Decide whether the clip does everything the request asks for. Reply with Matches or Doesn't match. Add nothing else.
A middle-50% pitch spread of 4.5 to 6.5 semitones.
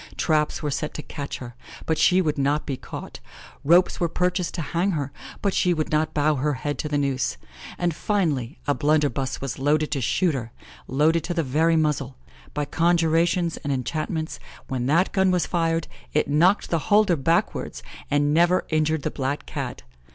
Doesn't match